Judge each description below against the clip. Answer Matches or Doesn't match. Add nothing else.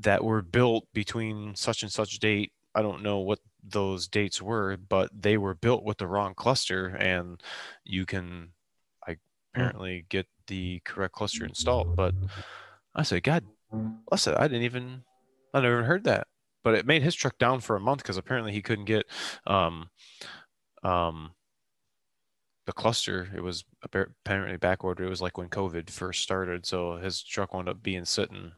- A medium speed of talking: Matches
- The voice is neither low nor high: Doesn't match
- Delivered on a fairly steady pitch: Doesn't match